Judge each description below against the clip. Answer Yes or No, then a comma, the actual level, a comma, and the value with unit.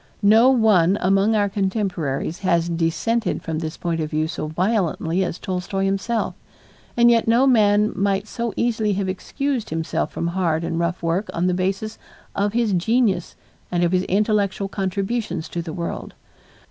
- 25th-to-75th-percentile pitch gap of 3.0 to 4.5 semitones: Yes, average, 4.0 semitones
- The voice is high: Yes, high, 195 Hz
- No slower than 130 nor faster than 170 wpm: Yes, average, 165 wpm